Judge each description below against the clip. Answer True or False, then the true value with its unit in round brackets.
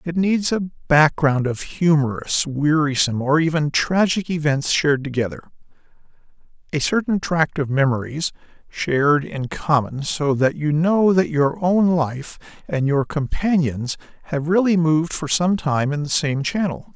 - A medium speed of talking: True (150 wpm)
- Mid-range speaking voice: True (155 Hz)